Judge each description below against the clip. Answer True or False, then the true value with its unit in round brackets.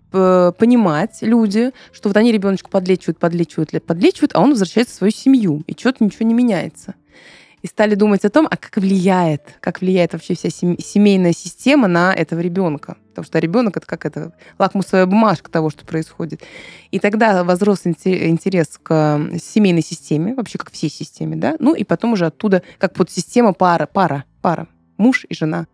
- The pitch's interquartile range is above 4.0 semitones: True (4.5 semitones)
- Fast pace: True (175 wpm)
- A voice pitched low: False (185 Hz)